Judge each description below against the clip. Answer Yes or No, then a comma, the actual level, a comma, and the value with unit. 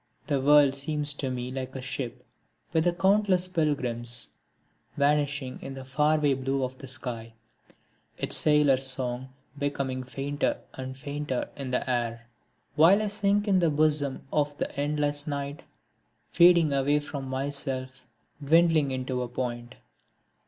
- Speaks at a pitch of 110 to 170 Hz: Yes, medium, 140 Hz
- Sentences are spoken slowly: No, average, 145 wpm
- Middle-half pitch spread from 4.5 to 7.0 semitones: No, narrow, 2.5 semitones